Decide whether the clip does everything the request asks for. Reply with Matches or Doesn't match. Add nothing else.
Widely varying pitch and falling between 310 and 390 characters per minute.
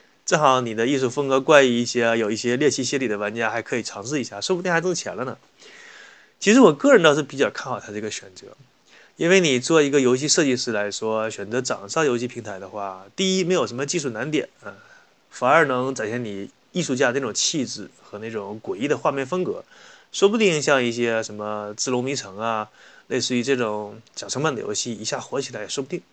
Matches